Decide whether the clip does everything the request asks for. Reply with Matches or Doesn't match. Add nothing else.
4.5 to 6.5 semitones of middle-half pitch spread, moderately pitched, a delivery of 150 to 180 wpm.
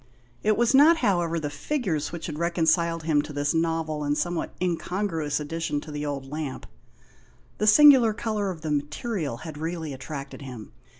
Doesn't match